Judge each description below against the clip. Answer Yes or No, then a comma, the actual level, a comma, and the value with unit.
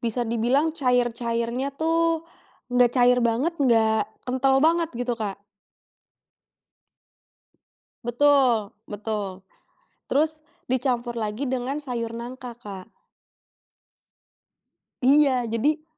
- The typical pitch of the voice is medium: No, high, 245 Hz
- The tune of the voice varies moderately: Yes, average, 3.1 semitones